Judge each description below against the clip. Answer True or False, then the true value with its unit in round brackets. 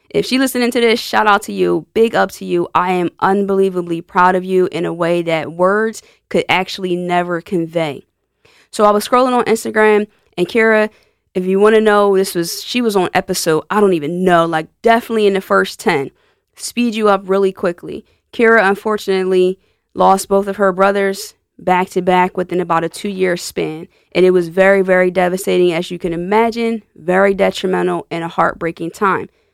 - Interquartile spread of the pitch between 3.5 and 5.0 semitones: False (2.7 semitones)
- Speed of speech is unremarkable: True (190 wpm)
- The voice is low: False (190 Hz)